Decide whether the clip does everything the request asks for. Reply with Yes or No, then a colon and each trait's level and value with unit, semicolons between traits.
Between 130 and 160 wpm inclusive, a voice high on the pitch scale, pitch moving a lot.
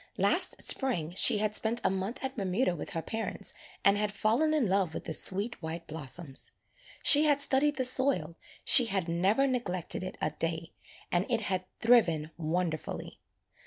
No: average, 170 wpm; high, 195 Hz; wide, 6.3 semitones